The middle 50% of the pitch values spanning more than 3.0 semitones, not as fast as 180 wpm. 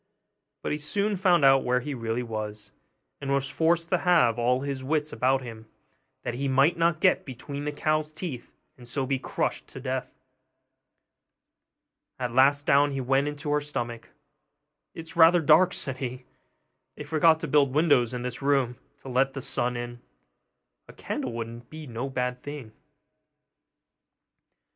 Yes: average, 3.5 semitones; average, 165 wpm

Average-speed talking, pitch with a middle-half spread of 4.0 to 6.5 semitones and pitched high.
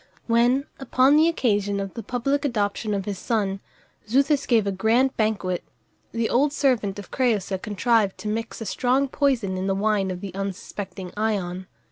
Yes: average, 170 wpm; average, 4.3 semitones; high, 215 Hz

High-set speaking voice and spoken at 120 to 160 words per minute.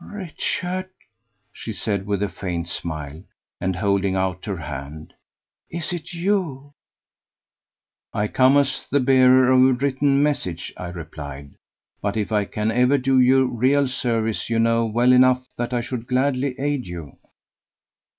No: low, 120 Hz; average, 150 wpm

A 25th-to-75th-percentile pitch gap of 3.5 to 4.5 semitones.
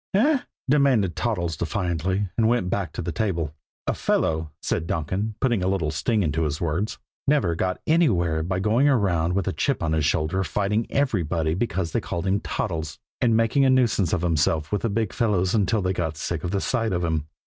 No: wide, 5.4 semitones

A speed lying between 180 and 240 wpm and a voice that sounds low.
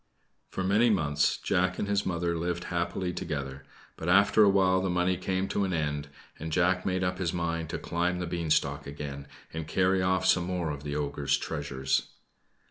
Yes: average, 190 wpm; very low, 85 Hz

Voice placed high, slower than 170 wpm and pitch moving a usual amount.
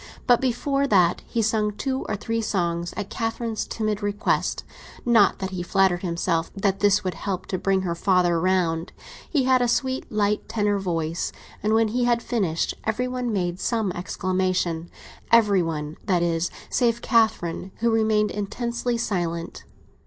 Yes: high, 205 Hz; average, 160 wpm; average, 4.4 semitones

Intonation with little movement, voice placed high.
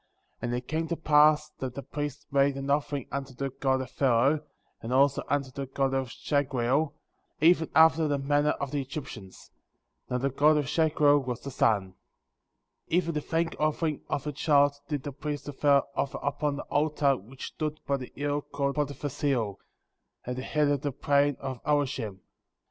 No: narrow, 2.0 semitones; medium, 140 Hz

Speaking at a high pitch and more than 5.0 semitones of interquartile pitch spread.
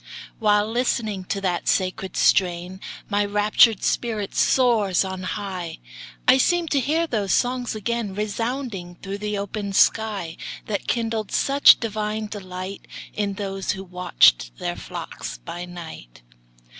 No: high, 205 Hz; average, 3.2 semitones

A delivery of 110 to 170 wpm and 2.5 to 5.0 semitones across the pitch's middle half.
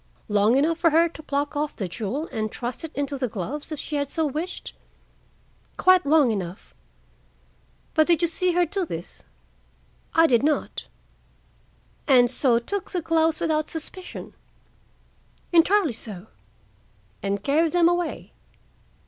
No: average, 150 wpm; wide, 5.4 semitones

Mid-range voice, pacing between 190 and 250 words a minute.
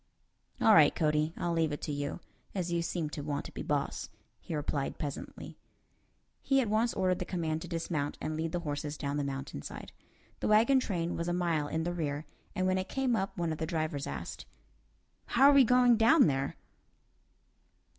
Yes: medium, 165 Hz; average, 200 wpm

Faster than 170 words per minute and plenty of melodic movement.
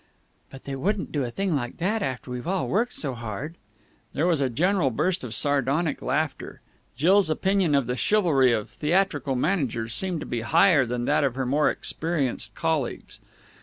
Yes: average, 180 wpm; wide, 5.8 semitones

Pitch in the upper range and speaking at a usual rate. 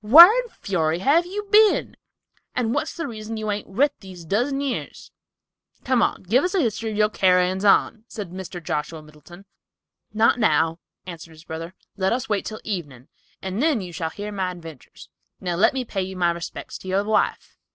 Yes: high, 200 Hz; average, 185 wpm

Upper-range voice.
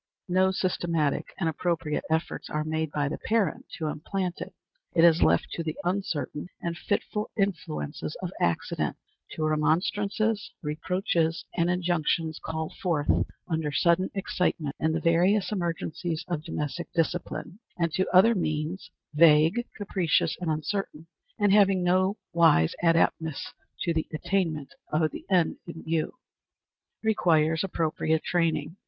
No: medium, 170 Hz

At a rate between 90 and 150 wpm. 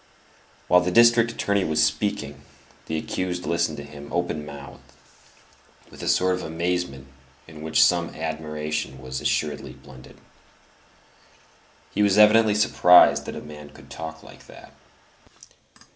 Yes: slow, 135 wpm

